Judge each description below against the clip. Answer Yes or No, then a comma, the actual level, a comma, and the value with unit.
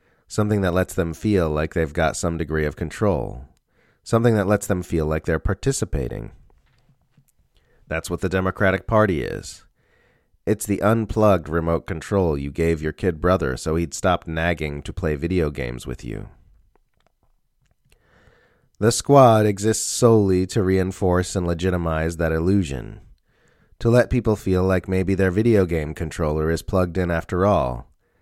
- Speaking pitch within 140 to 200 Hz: No, very low, 90 Hz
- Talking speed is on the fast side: No, average, 150 wpm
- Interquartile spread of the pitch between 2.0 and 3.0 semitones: No, average, 3.9 semitones